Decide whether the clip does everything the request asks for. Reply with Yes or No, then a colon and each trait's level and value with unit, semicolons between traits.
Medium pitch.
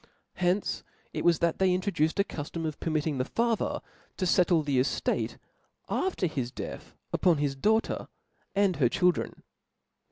Yes: medium, 170 Hz